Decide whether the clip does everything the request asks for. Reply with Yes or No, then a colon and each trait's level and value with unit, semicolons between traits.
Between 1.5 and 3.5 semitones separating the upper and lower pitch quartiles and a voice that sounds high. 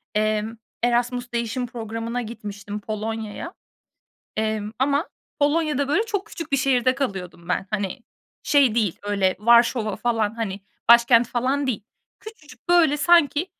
No: average, 4.4 semitones; high, 235 Hz